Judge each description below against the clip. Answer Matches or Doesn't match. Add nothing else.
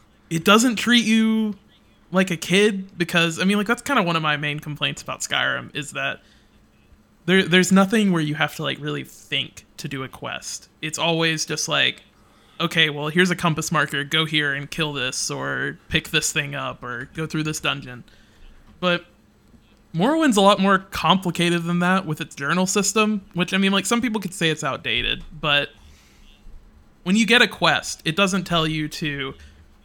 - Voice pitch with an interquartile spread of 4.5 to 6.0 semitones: Matches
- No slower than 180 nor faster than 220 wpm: Matches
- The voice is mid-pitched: Matches